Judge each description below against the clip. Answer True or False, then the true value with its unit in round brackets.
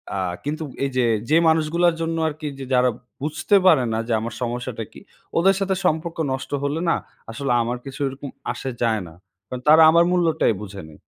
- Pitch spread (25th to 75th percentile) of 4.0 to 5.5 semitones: True (4.9 semitones)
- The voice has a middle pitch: True (145 Hz)